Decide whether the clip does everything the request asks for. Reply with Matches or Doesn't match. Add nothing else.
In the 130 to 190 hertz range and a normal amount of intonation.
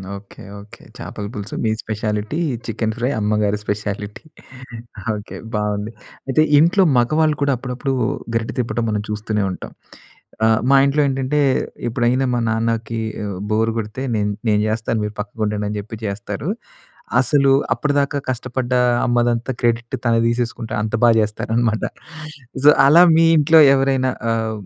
Doesn't match